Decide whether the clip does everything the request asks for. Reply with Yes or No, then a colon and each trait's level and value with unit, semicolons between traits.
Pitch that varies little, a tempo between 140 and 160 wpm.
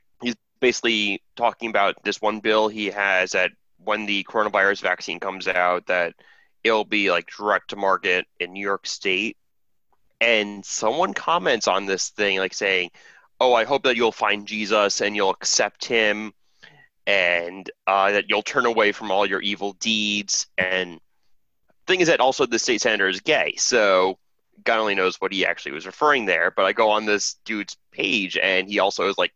No: narrow, 2.1 semitones; average, 180 wpm